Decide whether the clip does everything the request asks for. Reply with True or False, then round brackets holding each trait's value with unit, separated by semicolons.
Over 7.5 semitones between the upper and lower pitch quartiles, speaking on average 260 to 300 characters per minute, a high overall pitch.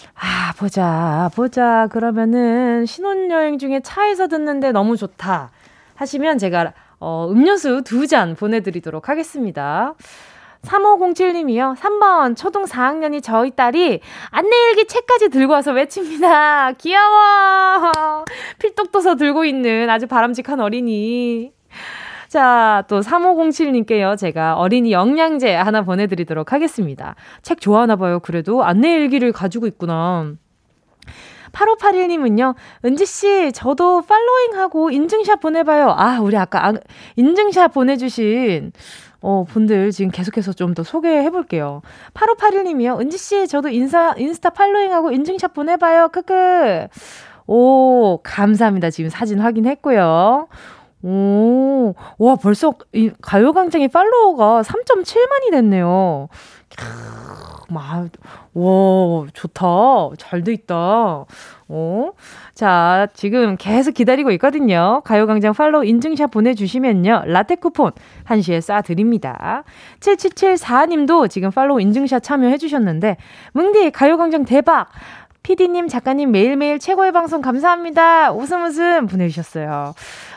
True (8.3 semitones; 270 characters per minute; 255 Hz)